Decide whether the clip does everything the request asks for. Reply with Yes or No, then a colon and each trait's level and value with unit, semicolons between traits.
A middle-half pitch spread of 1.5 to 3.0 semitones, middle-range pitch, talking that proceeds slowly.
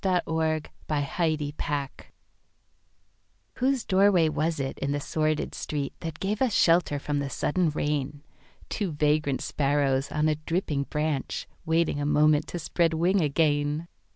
Yes: narrow, 2.4 semitones; medium, 155 Hz; slow, 130 wpm